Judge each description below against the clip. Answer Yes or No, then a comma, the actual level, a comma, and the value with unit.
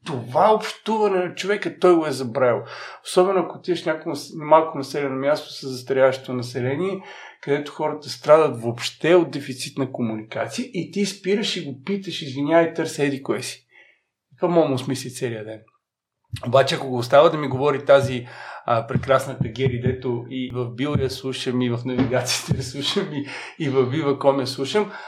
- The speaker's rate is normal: No, fast, 175 wpm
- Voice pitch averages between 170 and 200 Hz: No, medium, 140 Hz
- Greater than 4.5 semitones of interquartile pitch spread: No, average, 4.2 semitones